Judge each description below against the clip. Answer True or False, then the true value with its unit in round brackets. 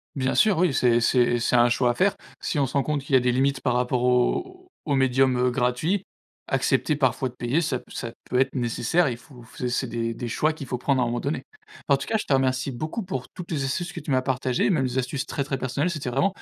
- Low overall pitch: True (130 Hz)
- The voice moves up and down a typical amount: True (3.2 semitones)